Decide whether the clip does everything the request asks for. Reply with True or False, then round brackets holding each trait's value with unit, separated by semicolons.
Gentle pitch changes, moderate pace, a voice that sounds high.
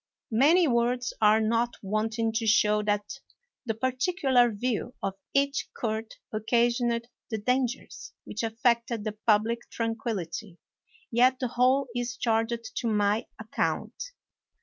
False (2.2 semitones; 125 wpm; 230 Hz)